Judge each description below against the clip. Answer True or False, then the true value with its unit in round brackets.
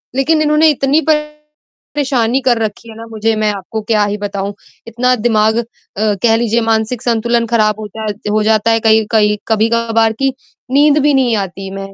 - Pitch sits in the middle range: False (225 Hz)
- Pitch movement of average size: True (3.3 semitones)